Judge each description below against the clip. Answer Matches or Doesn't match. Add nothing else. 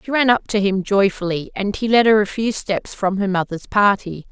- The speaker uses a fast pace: Matches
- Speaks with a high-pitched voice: Matches